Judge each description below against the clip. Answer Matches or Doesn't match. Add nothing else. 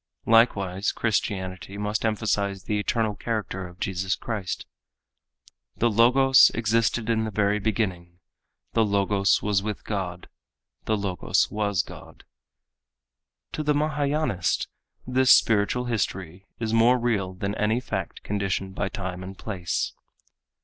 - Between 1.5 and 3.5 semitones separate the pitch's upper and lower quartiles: Matches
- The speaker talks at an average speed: Doesn't match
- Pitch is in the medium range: Doesn't match